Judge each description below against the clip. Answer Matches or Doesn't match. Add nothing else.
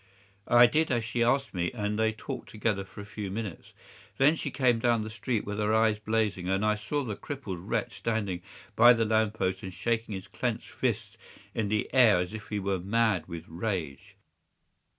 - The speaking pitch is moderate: Doesn't match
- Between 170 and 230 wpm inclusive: Matches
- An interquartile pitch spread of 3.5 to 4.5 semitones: Doesn't match